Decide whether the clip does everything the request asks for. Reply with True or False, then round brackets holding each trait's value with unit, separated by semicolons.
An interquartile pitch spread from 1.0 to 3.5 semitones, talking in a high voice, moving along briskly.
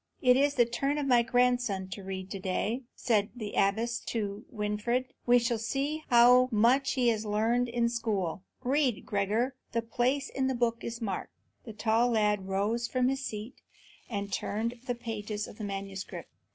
False (3.0 semitones; 230 Hz; 180 wpm)